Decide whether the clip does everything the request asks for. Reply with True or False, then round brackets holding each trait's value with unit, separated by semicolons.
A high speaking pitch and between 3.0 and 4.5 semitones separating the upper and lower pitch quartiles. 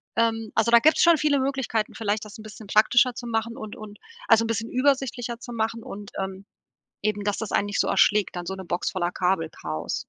False (220 Hz; 2.6 semitones)